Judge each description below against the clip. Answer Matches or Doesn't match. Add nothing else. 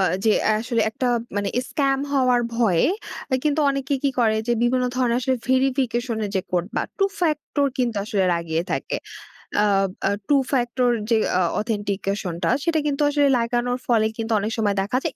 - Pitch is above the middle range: Matches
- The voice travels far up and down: Doesn't match